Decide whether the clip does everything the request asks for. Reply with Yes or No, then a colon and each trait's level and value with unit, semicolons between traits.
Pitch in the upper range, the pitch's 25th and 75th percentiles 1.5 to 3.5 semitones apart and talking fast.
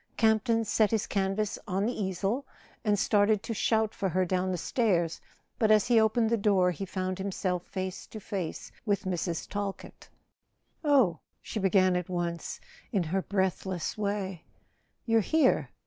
No: high, 200 Hz; average, 2.9 semitones; average, 160 wpm